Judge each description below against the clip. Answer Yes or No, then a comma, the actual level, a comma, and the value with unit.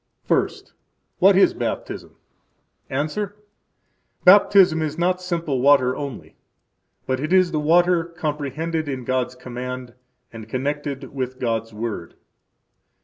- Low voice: No, medium, 145 Hz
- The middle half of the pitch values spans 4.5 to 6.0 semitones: Yes, average, 4.8 semitones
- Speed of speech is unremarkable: No, slow, 115 wpm